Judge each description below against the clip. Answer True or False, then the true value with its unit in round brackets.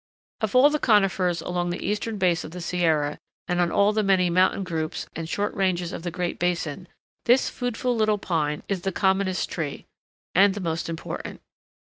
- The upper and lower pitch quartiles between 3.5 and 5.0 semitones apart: False (3.1 semitones)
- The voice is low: False (180 Hz)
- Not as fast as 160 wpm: False (190 wpm)